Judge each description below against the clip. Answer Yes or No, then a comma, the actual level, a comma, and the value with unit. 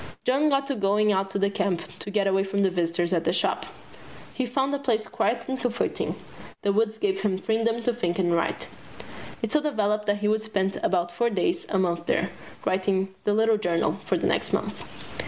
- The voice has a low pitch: No, high, 205 Hz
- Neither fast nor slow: No, fast, 210 wpm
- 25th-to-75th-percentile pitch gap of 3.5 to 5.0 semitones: No, average, 3.1 semitones